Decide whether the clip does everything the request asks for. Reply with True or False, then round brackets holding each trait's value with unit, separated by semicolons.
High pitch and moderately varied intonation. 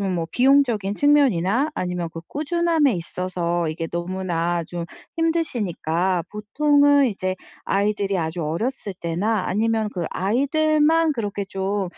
False (200 Hz; 8.1 semitones)